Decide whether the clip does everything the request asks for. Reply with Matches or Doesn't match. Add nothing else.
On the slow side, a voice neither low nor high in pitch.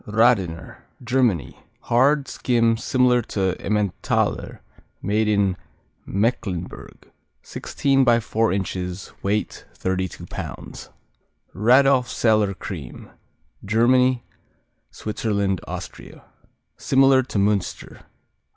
Doesn't match